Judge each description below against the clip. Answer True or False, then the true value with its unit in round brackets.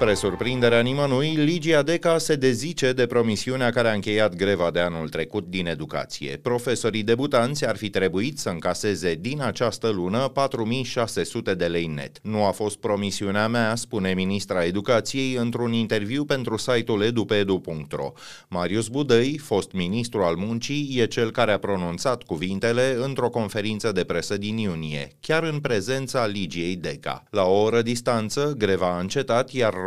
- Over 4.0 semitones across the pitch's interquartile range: True (4.6 semitones)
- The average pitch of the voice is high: False (115 Hz)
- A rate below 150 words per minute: False (155 wpm)